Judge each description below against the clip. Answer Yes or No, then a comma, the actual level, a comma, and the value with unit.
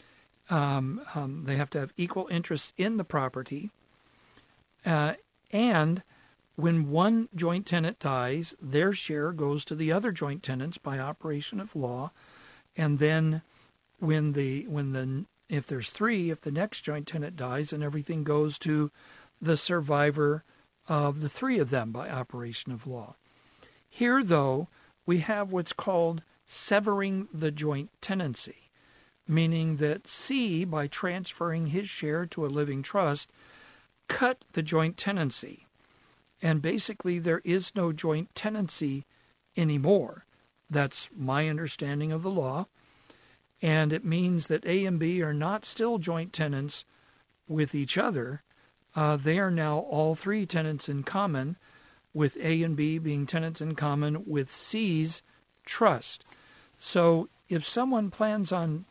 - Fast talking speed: No, average, 140 wpm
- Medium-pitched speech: Yes, medium, 160 Hz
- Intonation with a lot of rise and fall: No, average, 3.5 semitones